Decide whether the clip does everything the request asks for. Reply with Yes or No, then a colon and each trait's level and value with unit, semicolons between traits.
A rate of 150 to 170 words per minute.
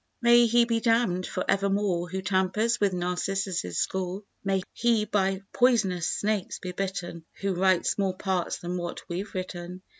Yes: average, 155 wpm